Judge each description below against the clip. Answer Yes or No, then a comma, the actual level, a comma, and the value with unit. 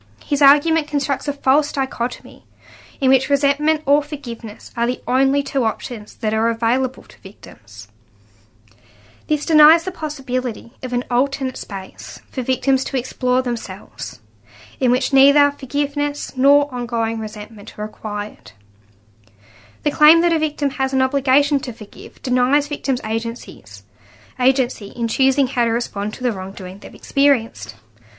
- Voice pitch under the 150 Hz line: No, very high, 250 Hz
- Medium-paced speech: Yes, average, 145 wpm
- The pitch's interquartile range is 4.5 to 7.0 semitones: Yes, wide, 5.6 semitones